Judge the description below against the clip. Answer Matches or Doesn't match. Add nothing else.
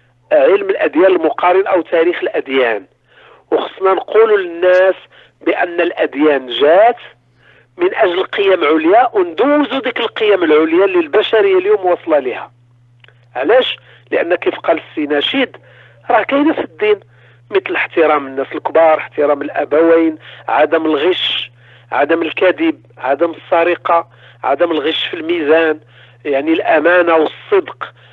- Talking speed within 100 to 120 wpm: Matches